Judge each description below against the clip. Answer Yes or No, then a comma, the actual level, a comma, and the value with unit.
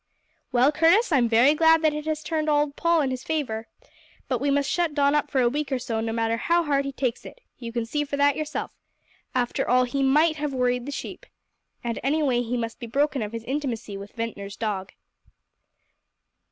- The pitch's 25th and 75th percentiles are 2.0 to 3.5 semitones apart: No, average, 4.2 semitones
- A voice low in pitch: No, very high, 275 Hz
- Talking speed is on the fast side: Yes, fast, 210 wpm